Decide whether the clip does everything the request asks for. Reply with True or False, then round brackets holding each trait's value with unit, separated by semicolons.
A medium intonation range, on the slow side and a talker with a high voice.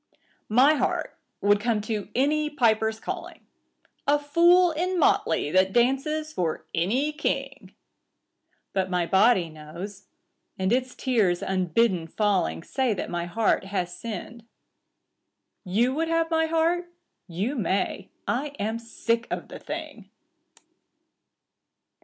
False (7.4 semitones; 125 wpm; 230 Hz)